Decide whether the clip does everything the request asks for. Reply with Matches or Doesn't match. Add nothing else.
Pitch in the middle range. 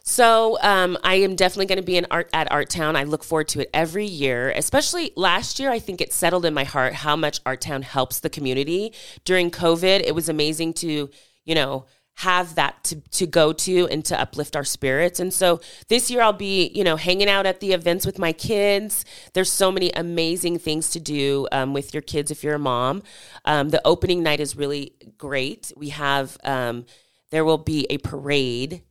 Matches